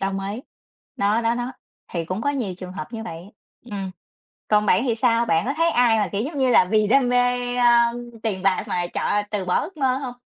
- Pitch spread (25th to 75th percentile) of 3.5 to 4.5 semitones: Yes, average, 4.1 semitones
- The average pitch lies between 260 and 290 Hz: No, high, 225 Hz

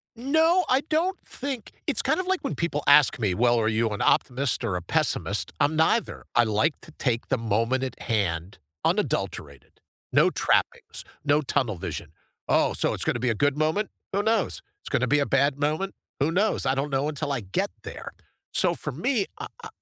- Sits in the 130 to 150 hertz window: Yes, medium, 140 Hz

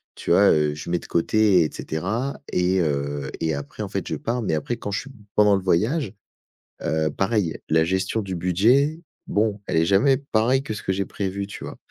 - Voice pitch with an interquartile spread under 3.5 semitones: No, average, 5.0 semitones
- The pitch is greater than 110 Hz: No, very low, 95 Hz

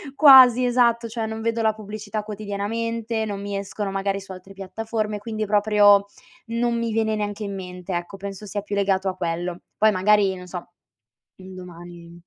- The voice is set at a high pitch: Yes, high, 205 Hz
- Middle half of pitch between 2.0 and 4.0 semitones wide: Yes, narrow, 2.4 semitones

